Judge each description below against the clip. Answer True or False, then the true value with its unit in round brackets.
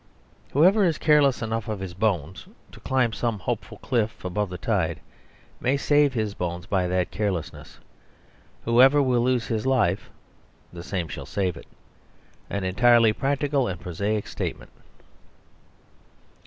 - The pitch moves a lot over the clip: True (5.8 semitones)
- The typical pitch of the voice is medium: False (110 Hz)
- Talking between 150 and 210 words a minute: False (140 wpm)